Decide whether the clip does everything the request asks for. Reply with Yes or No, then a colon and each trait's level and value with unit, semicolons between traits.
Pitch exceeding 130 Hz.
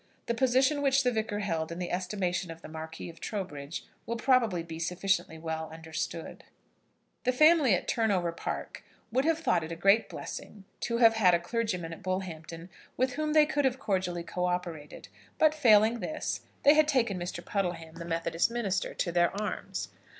Yes: high, 190 Hz